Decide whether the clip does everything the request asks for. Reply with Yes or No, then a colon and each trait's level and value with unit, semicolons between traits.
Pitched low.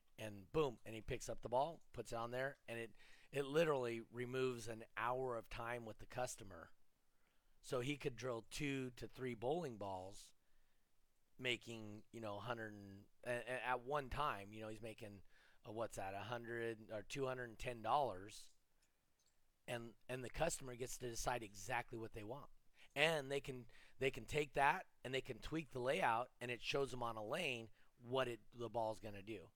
Yes: low, 120 Hz